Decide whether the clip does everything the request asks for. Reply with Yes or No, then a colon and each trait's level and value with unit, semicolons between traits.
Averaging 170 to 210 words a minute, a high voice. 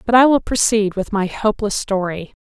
Yes: average, 200 wpm; high, 210 Hz